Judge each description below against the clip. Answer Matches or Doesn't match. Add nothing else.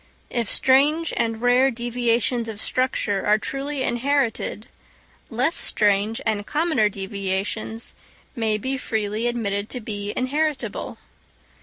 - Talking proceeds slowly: Matches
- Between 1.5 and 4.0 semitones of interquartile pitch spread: Matches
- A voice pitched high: Matches